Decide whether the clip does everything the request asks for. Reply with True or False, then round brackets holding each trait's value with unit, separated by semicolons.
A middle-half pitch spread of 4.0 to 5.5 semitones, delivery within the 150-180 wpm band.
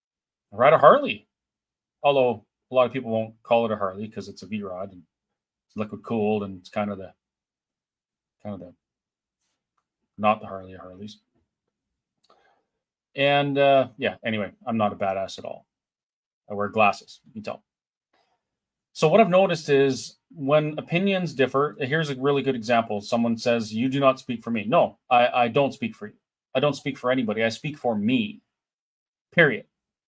True (5.2 semitones; 175 wpm)